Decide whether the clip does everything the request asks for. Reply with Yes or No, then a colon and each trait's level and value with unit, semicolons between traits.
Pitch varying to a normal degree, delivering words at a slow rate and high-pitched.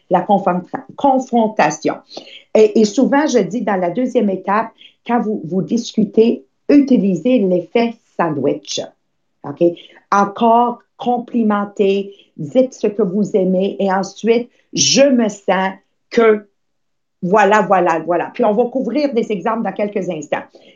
Yes: average, 3.6 semitones; slow, 125 wpm; high, 215 Hz